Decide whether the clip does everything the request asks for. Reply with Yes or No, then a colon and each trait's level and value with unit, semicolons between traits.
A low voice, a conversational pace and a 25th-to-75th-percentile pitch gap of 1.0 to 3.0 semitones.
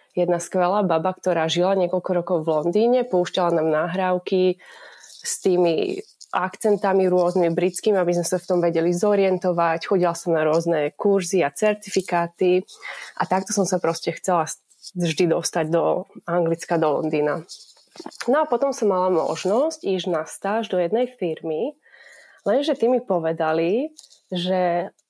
No: medium, 180 Hz; average, 140 wpm; narrow, 2.5 semitones